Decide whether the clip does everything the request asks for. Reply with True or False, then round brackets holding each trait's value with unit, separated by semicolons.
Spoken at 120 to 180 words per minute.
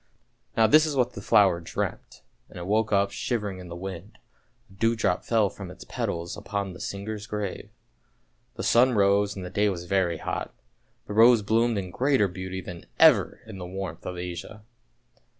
False (195 wpm)